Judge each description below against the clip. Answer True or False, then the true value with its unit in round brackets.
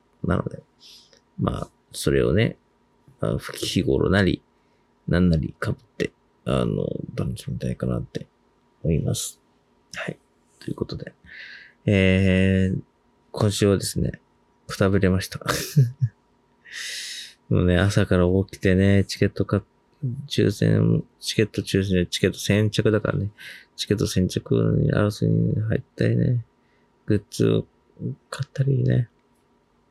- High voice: False (105 Hz)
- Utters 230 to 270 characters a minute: True (235 characters per minute)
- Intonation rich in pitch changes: False (5.0 semitones)